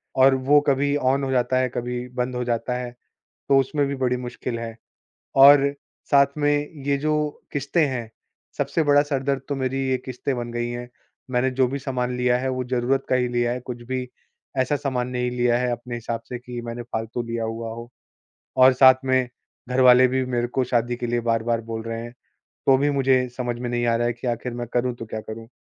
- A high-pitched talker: No, low, 125 Hz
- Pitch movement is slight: Yes, narrow, 1.8 semitones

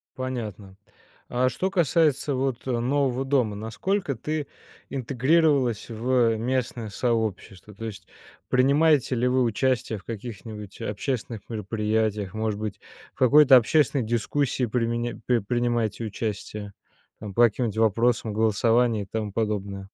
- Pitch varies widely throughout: No, average, 3.3 semitones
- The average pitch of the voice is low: Yes, low, 115 Hz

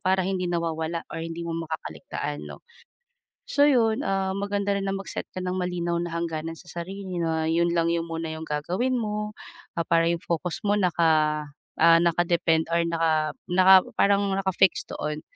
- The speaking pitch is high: No, medium, 170 Hz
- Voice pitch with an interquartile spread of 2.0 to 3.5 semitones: Yes, average, 2.7 semitones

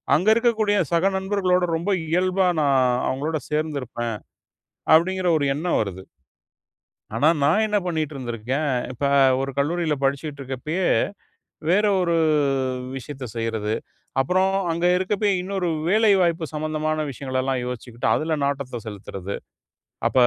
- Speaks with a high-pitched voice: No, medium, 155 Hz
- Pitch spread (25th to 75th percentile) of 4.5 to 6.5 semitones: Yes, wide, 5.6 semitones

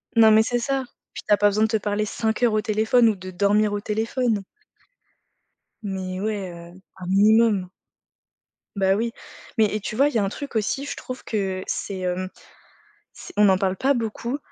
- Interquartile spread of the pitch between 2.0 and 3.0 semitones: Yes, average, 2.7 semitones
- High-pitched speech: Yes, high, 215 Hz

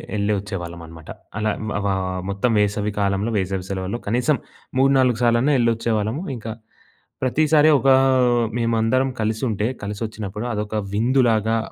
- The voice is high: No, low, 110 Hz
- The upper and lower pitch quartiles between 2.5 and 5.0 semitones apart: Yes, average, 2.8 semitones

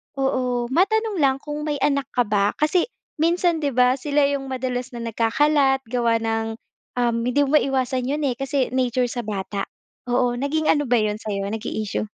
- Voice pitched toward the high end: Yes, very high, 255 Hz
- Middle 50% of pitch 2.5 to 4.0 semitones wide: Yes, average, 3.6 semitones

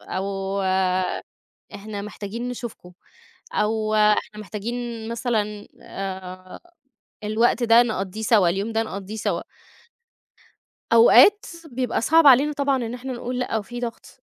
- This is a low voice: No, high, 220 Hz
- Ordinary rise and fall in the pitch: Yes, average, 3.1 semitones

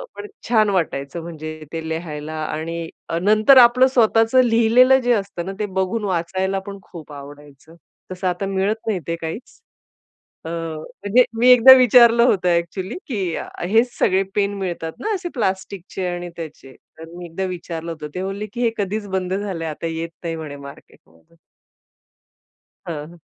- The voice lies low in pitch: No, medium, 185 Hz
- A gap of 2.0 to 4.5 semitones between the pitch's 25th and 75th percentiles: No, average, 4.9 semitones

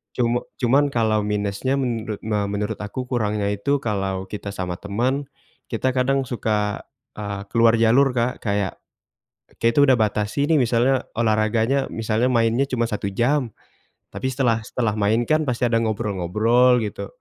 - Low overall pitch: Yes, low, 115 Hz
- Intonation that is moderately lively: Yes, average, 3.4 semitones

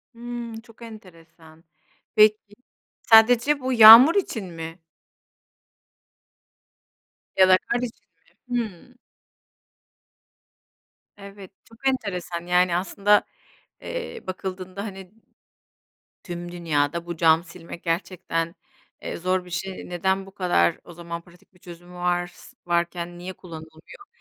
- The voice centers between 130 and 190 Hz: Yes, medium, 185 Hz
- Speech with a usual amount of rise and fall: Yes, average, 4.0 semitones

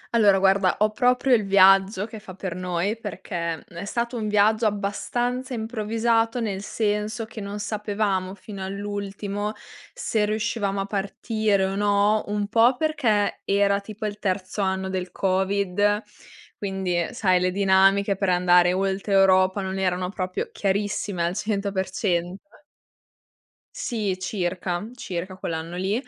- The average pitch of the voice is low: No, high, 200 Hz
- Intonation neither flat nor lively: No, narrow, 2.2 semitones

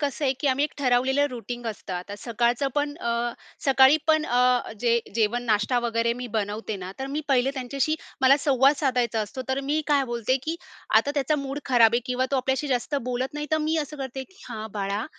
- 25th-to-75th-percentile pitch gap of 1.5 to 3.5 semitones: Yes, average, 3.0 semitones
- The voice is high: Yes, very high, 255 Hz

